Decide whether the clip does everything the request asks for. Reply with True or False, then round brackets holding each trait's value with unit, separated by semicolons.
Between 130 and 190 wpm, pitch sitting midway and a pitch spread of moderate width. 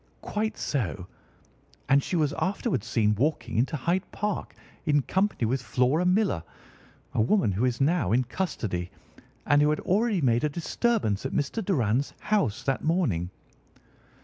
False (150 wpm; 145 Hz; 7.8 semitones)